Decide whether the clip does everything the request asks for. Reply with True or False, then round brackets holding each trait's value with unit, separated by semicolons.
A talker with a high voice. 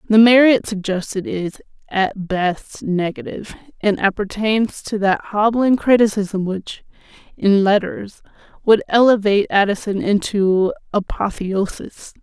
True (205 Hz)